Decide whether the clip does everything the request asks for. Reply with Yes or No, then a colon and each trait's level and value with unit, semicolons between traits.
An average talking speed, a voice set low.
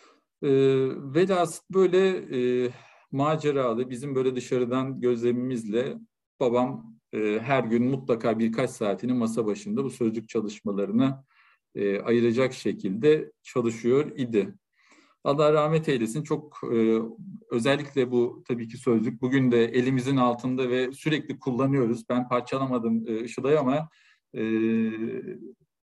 Yes: average, 115 wpm; low, 125 Hz